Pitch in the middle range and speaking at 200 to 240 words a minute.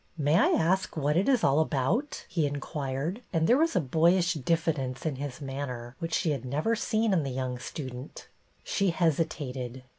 Yes: medium, 150 Hz; fast, 205 wpm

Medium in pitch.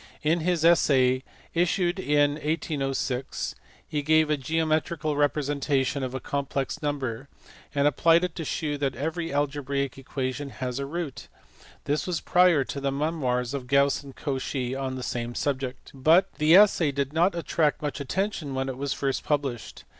Yes: medium, 145 Hz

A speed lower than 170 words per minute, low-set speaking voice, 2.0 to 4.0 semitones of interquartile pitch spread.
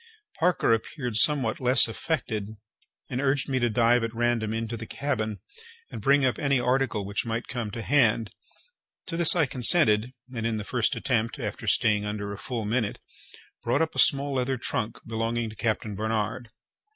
No: average, 175 wpm; low, 115 Hz; average, 3.2 semitones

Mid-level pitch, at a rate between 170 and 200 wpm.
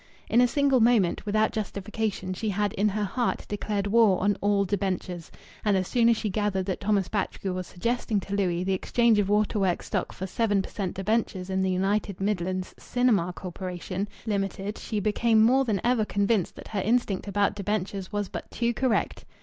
No: high, 205 Hz; average, 190 wpm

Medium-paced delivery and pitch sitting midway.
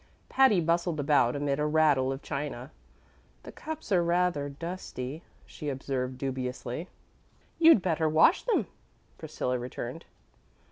No: slow, 125 wpm; medium, 150 Hz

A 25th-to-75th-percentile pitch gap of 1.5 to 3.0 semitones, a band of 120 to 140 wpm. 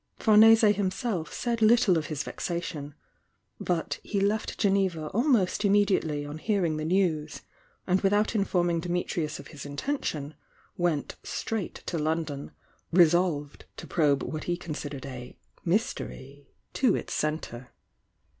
No: average, 5.0 semitones; slow, 135 wpm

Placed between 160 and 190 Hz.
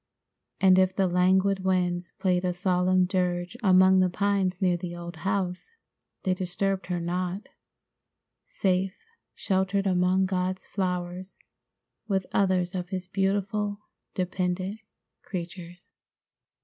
Yes: medium, 185 Hz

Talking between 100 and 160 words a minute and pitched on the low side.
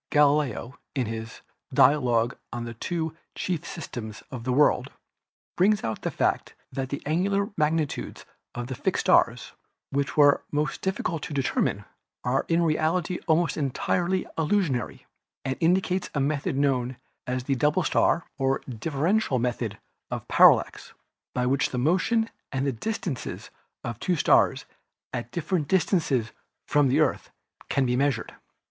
No: average, 145 wpm; medium, 145 Hz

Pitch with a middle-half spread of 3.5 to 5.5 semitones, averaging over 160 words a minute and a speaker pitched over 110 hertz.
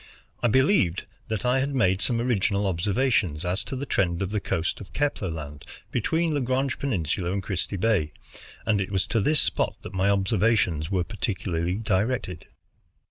No: average, 5.2 semitones; average, 170 wpm; low, 100 Hz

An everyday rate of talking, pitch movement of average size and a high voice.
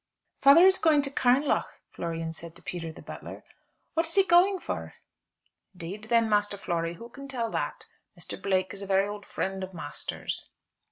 No: average, 180 wpm; wide, 7.6 semitones; high, 205 Hz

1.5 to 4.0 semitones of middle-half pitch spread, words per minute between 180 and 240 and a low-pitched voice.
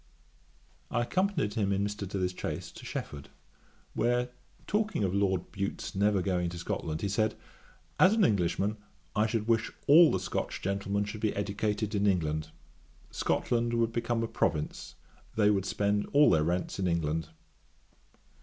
No: average, 3.6 semitones; average, 155 wpm; low, 100 Hz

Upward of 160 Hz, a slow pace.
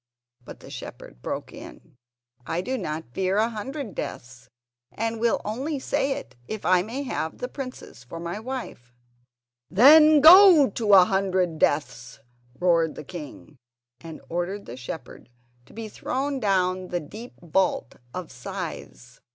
No: high, 190 Hz; average, 160 wpm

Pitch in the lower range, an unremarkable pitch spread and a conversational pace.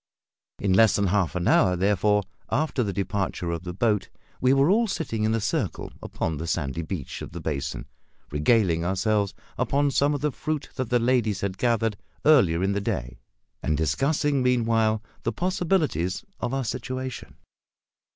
No: low, 105 Hz; wide, 6.2 semitones; average, 170 wpm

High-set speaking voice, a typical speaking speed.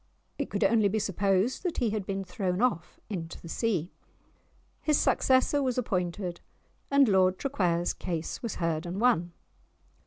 Yes: high, 195 Hz; average, 155 wpm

